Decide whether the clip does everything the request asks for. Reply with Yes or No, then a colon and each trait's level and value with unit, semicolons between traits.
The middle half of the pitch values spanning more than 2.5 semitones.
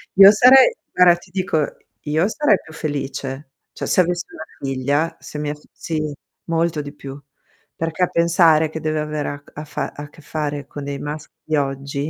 Yes: average, 2.9 semitones